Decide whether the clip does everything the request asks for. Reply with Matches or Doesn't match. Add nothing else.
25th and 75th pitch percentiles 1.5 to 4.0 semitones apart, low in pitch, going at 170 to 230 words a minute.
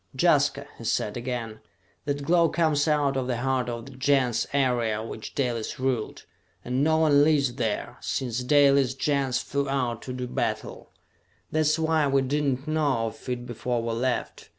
Matches